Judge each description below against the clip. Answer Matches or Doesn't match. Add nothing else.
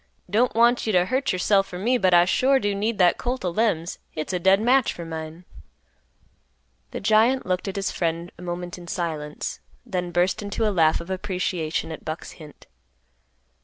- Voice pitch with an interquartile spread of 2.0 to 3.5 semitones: Doesn't match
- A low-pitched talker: Doesn't match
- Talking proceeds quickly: Doesn't match